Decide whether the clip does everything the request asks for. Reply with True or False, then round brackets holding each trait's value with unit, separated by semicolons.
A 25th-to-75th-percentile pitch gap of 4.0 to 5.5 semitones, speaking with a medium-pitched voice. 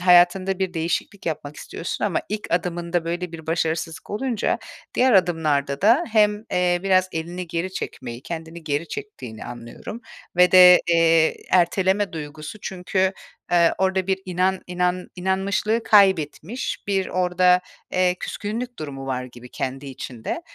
False (2.9 semitones; 180 Hz)